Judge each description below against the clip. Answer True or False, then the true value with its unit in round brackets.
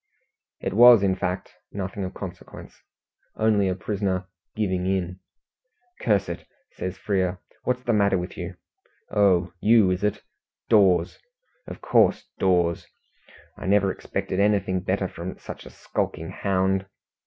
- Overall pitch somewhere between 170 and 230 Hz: False (95 Hz)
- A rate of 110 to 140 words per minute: True (135 wpm)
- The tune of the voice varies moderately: False (1.8 semitones)